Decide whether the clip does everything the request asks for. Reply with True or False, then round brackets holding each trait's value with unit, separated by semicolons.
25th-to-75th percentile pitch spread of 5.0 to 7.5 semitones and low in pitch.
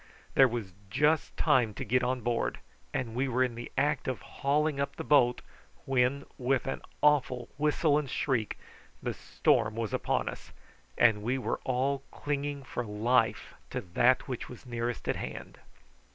False (2.8 semitones; 130 Hz)